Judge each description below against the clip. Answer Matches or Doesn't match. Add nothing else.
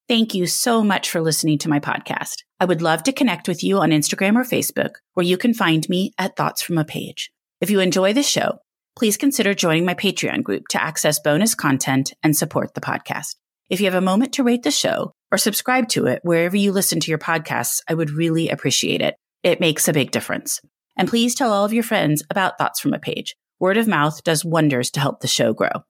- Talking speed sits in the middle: Doesn't match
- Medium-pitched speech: Matches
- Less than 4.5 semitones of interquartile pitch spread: Doesn't match